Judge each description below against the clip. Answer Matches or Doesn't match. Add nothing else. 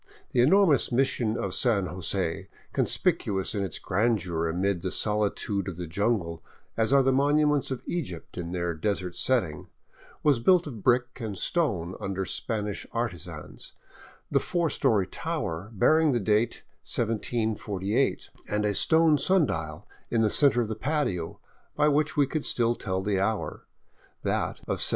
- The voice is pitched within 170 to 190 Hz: Doesn't match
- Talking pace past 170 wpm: Doesn't match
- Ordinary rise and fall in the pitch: Doesn't match